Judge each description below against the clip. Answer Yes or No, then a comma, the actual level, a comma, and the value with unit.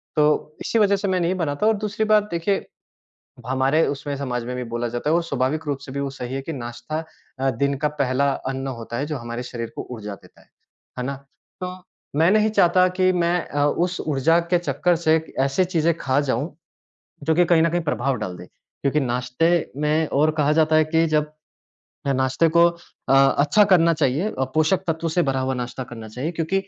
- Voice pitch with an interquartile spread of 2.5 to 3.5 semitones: No, average, 4.3 semitones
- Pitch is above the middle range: No, medium, 150 Hz